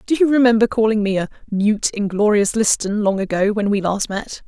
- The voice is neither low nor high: No, high, 210 Hz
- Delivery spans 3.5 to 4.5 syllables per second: No, 5.4 syllables/s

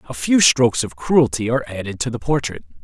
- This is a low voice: Yes, low, 120 Hz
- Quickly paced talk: Yes, fast, 210 wpm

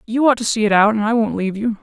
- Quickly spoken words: Yes, fast, 360 wpm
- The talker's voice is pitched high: Yes, high, 220 Hz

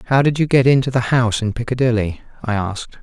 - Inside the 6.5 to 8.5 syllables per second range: Yes, 6.6 syllables/s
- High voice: No, low, 120 Hz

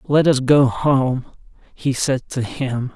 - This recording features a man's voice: Yes, male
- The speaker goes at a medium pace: Yes, average, 165 wpm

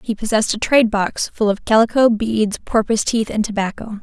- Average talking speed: Yes, average, 195 wpm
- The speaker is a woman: Yes, female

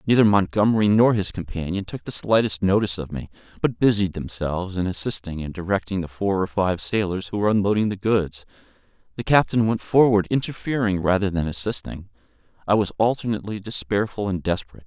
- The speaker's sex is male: Yes, male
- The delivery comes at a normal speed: Yes, average, 170 wpm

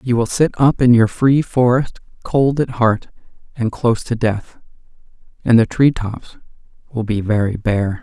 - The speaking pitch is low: Yes, low, 120 Hz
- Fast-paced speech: No, average, 170 wpm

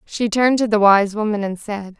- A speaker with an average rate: No, fast, 240 wpm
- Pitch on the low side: No, high, 210 Hz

